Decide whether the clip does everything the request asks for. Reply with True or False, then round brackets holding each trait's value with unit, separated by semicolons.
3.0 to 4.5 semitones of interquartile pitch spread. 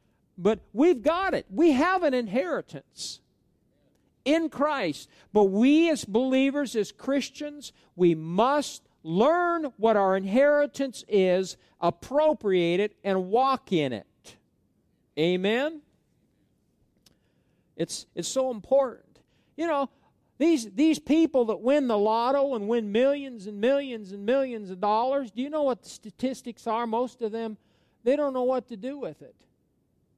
False (5.1 semitones)